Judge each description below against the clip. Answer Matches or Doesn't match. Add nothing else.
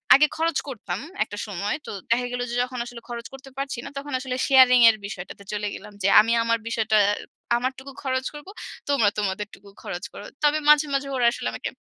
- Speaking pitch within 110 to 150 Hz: Doesn't match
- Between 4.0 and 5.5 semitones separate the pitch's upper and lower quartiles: Matches